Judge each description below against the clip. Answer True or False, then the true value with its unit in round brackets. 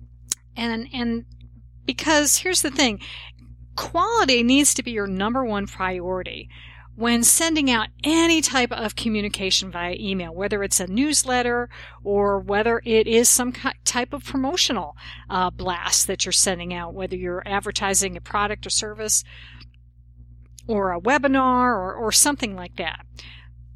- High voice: True (205 Hz)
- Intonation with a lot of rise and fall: True (5.9 semitones)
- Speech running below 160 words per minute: True (140 wpm)